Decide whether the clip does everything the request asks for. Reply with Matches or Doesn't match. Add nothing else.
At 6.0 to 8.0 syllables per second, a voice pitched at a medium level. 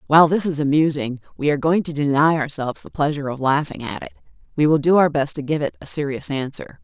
Matches